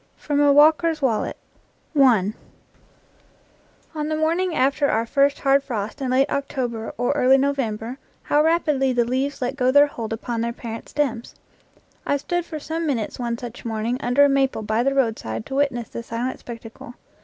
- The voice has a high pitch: Yes, very high, 265 Hz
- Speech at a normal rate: Yes, average, 170 wpm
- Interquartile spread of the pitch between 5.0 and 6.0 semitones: No, average, 3.5 semitones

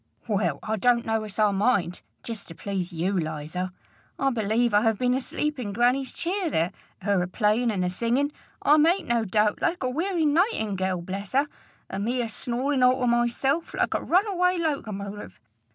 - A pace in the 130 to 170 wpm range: No, average, 185 wpm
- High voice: Yes, high, 235 Hz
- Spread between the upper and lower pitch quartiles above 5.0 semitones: Yes, wide, 5.5 semitones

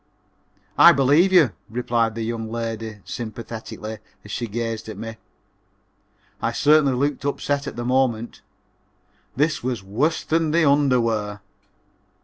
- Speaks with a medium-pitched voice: No, low, 120 Hz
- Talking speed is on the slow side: Yes, slow, 130 wpm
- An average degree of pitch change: Yes, average, 4.0 semitones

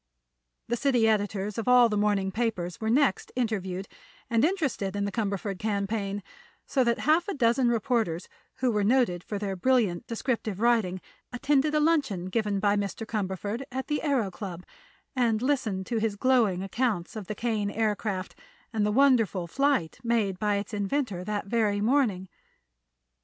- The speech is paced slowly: No, average, 165 wpm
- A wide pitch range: No, average, 3.7 semitones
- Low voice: No, high, 215 Hz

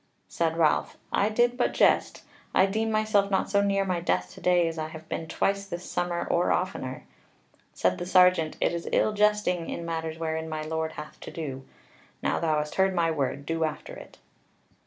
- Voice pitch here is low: No, medium, 170 Hz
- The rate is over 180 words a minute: Yes, average, 200 wpm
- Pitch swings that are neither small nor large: Yes, average, 3.6 semitones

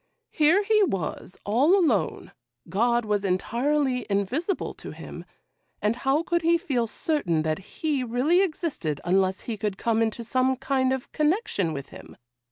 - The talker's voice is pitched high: Yes, very high, 250 Hz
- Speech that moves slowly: No, average, 155 wpm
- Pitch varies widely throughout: Yes, wide, 7.1 semitones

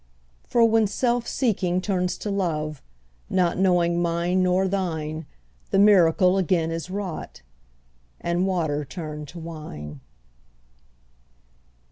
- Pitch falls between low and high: Yes, medium, 180 Hz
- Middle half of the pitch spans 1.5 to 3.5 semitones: Yes, average, 3.0 semitones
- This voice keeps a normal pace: No, slow, 110 wpm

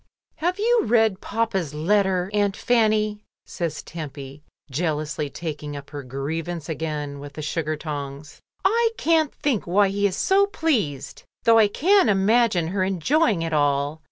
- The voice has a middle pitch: Yes, medium, 180 Hz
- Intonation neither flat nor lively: No, wide, 6.8 semitones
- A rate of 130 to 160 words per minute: Yes, average, 150 wpm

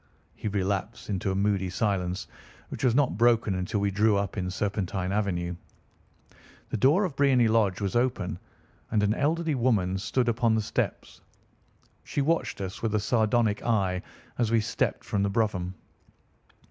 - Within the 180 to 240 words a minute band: No, average, 160 wpm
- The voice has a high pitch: No, low, 105 Hz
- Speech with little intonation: No, average, 3.6 semitones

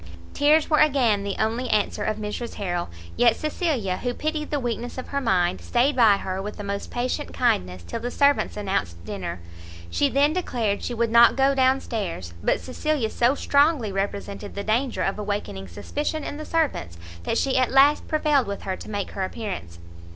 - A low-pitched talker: No, high, 235 Hz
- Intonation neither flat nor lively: No, wide, 5.8 semitones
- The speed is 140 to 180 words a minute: No, average, 190 wpm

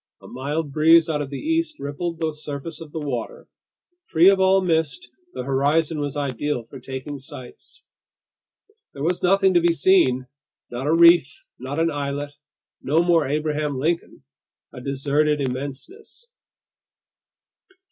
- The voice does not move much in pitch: No, average, 3.3 semitones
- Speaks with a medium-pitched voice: Yes, medium, 150 Hz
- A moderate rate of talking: Yes, average, 145 wpm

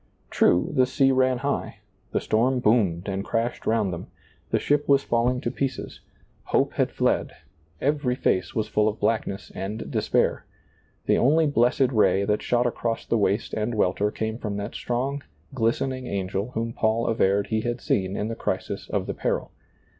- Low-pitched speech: Yes, low, 115 Hz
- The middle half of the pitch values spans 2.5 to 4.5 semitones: Yes, average, 3.6 semitones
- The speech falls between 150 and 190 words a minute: Yes, average, 175 wpm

